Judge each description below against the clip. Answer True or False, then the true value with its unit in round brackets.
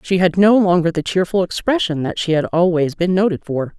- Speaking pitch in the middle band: True (175 Hz)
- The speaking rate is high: True (220 wpm)